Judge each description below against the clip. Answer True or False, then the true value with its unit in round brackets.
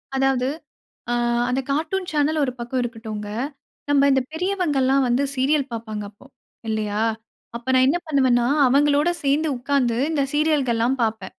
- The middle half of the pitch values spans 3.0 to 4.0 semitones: True (3.6 semitones)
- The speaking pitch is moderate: False (265 Hz)